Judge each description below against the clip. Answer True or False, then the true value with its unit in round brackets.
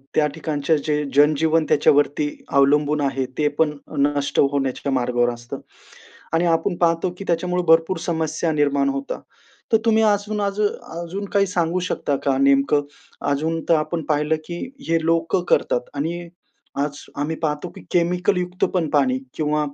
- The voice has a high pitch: False (155 Hz)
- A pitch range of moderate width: True (3.3 semitones)